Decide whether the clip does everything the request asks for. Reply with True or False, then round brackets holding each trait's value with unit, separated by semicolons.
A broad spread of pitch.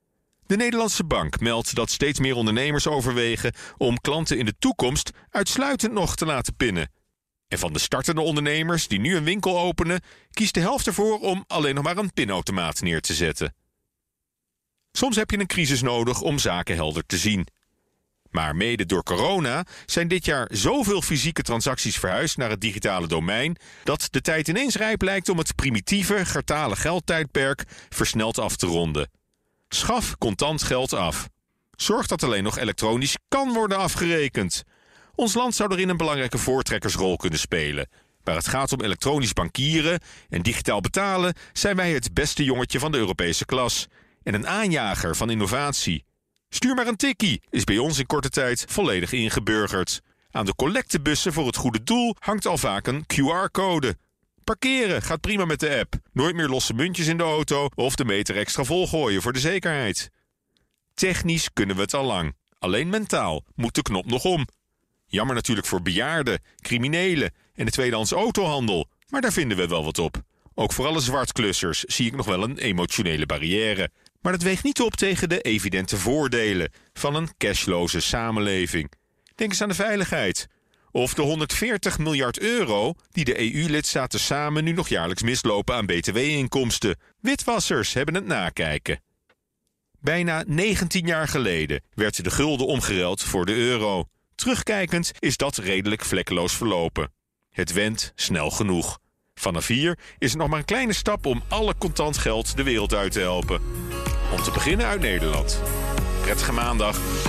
True (8.6 semitones)